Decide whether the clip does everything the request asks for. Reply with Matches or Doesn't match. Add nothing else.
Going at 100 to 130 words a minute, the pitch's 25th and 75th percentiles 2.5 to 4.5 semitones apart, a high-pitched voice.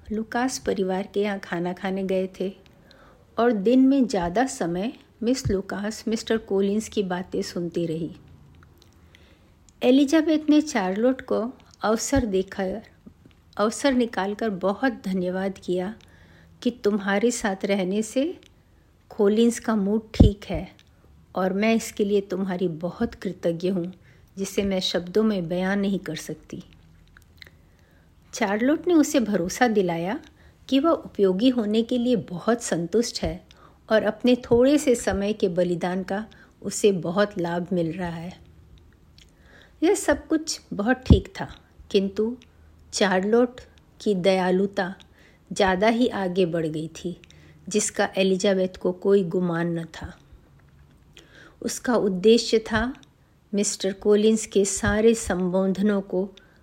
Matches